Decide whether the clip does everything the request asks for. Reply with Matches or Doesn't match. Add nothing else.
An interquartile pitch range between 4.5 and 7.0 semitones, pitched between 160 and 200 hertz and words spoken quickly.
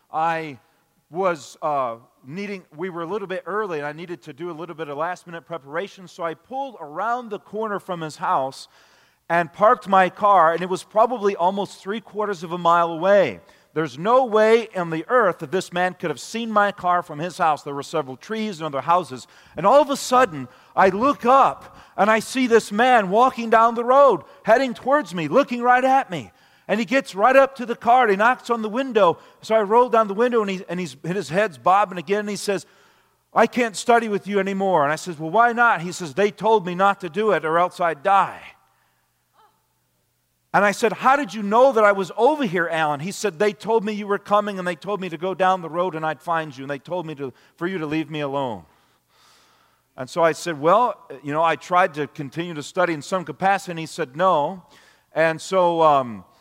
Matches